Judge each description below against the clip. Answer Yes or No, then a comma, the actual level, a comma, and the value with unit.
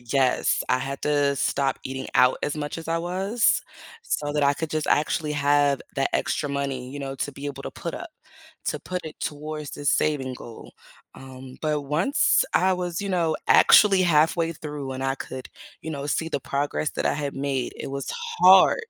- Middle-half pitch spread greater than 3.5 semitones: No, average, 2.8 semitones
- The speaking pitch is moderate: Yes, medium, 145 Hz